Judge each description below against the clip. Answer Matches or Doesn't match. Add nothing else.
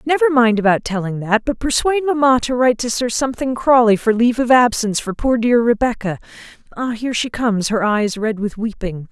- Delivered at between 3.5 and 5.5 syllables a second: Doesn't match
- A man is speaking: Doesn't match